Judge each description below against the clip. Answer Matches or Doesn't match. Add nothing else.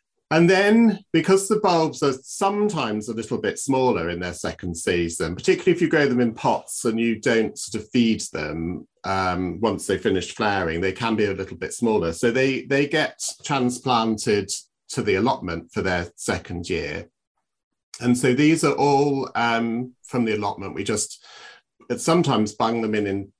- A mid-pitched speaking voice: Doesn't match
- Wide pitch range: Matches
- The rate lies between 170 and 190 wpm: Matches